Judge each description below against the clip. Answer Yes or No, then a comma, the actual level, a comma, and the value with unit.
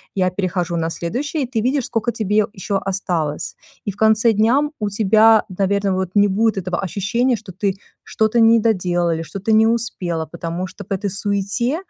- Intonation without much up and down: No, average, 3.4 semitones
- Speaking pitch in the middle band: No, high, 200 Hz